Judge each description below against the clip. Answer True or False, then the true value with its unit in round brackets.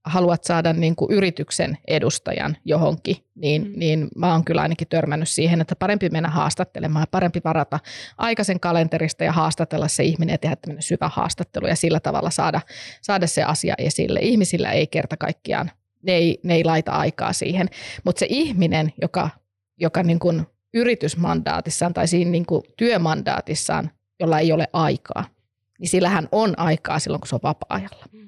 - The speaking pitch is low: False (165 Hz)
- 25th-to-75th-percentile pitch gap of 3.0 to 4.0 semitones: False (2.5 semitones)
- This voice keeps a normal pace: False (160 wpm)